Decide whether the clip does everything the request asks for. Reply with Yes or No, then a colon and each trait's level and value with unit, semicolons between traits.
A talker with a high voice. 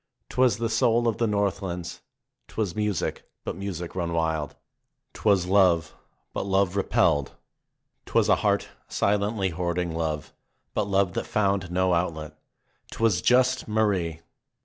No: very low, 95 Hz